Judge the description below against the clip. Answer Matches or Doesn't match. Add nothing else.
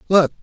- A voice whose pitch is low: Doesn't match